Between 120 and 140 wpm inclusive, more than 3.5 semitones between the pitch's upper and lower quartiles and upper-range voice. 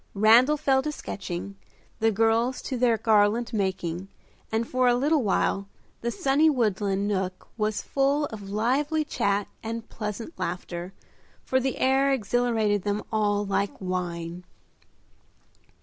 Yes: slow, 135 wpm; average, 4.4 semitones; high, 220 Hz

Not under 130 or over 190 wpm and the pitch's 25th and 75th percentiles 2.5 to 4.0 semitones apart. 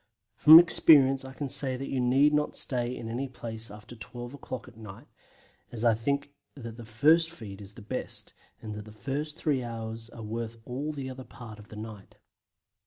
No: average, 200 wpm; average, 3.6 semitones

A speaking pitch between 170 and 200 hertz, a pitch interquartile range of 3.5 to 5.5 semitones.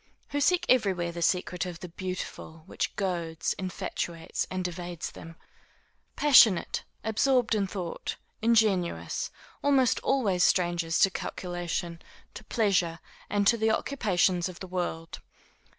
Yes: medium, 185 Hz; average, 4.1 semitones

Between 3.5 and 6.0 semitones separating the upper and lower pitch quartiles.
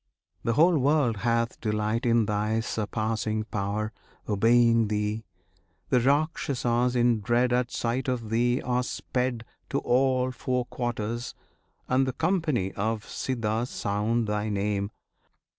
No: average, 2.7 semitones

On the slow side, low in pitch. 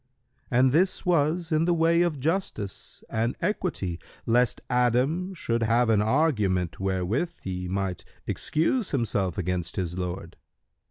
Yes: slow, 130 wpm; low, 120 Hz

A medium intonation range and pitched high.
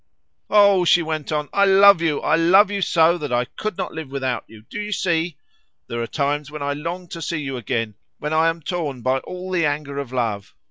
No: average, 4.3 semitones; medium, 155 Hz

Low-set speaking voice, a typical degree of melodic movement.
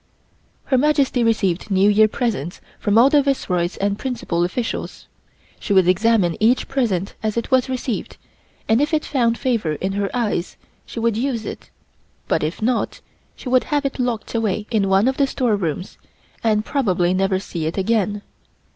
No: high, 220 Hz; average, 4.5 semitones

